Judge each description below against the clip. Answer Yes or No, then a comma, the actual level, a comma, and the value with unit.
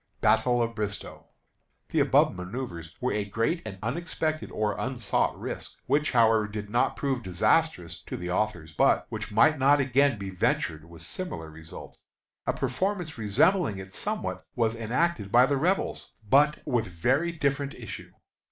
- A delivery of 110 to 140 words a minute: No, average, 155 wpm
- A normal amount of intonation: No, wide, 5.9 semitones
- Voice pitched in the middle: No, low, 115 Hz